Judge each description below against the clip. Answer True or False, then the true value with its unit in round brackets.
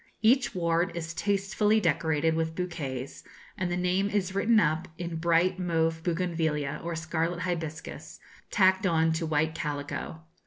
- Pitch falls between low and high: True (170 Hz)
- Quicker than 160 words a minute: False (145 wpm)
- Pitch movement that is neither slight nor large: False (2.3 semitones)